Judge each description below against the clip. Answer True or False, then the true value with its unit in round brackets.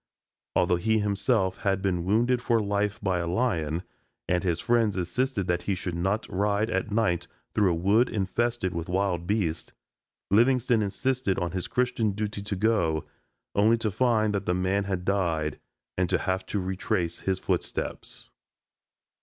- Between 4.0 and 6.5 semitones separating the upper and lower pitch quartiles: False (3.5 semitones)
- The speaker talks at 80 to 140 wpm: False (160 wpm)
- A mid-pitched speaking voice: False (100 Hz)